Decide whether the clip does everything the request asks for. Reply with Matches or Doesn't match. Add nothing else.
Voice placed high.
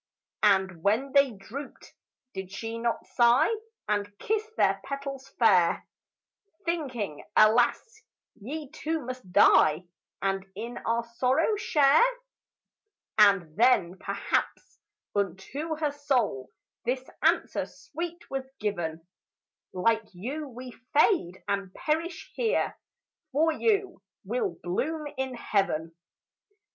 Matches